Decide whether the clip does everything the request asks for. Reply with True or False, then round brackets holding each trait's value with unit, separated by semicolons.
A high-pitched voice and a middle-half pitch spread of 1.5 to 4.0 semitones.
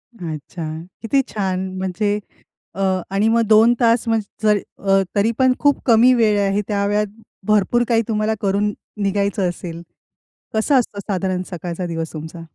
True (205 Hz; 3.1 semitones)